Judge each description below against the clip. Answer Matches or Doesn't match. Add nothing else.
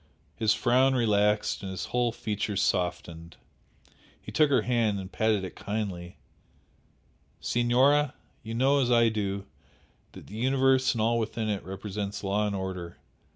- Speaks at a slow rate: Doesn't match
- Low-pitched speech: Matches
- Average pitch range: Matches